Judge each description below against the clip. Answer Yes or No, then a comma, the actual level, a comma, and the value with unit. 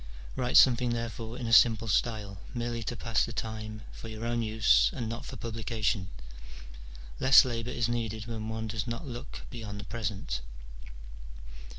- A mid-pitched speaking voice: No, low, 115 Hz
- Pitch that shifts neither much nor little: No, narrow, 1.6 semitones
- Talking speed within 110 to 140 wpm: No, average, 165 wpm